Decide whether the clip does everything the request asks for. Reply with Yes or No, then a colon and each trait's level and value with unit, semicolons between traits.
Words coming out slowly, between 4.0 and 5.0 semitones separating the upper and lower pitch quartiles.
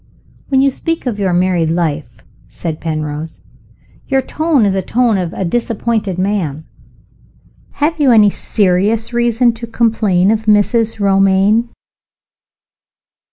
Yes: slow, 125 wpm; average, 4.4 semitones